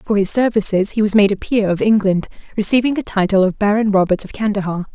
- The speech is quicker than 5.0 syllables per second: Yes, 6.2 syllables/s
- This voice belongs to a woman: Yes, female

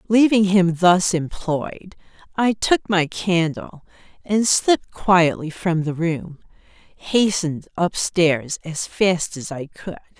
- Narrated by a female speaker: Yes, female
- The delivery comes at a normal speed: No, slow, 130 wpm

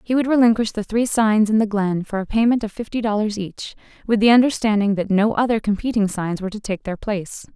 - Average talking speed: No, fast, 230 wpm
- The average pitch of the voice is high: Yes, high, 215 Hz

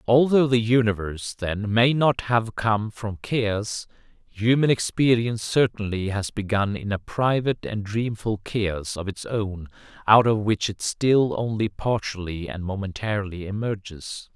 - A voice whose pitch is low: Yes, low, 110 Hz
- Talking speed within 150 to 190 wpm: No, average, 140 wpm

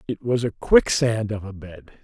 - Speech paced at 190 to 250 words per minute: Yes, fast, 205 wpm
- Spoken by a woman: No, male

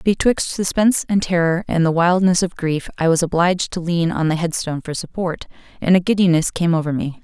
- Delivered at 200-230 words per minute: Yes, fast, 205 wpm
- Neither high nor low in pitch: Yes, medium, 175 Hz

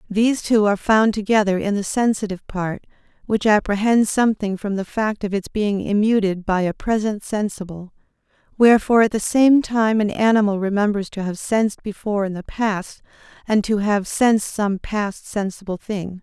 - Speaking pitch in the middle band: No, high, 205 Hz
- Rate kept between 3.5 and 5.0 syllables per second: No, 5.2 syllables/s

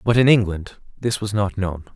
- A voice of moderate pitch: No, low, 105 Hz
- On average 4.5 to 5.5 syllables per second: Yes, 5.0 syllables/s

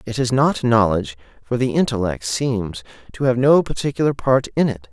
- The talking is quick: No, average, 185 wpm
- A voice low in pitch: Yes, low, 120 Hz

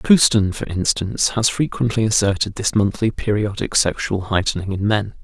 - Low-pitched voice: Yes, low, 105 Hz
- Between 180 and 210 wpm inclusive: No, average, 150 wpm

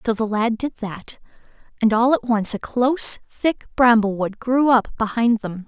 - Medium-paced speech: Yes, average, 180 wpm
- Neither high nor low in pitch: No, high, 230 Hz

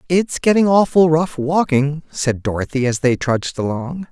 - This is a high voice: No, medium, 150 Hz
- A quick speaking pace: No, average, 160 wpm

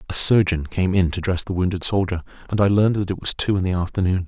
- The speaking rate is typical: No, fast, 265 wpm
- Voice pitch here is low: Yes, very low, 95 Hz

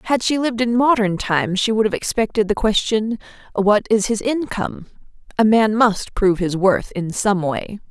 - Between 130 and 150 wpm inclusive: No, average, 190 wpm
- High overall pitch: Yes, high, 215 Hz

